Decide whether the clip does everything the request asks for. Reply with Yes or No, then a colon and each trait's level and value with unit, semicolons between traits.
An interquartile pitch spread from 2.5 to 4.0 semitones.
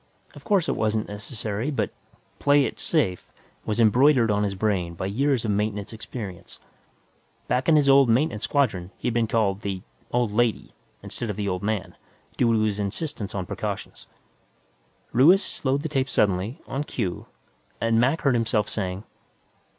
No: average, 4.7 semitones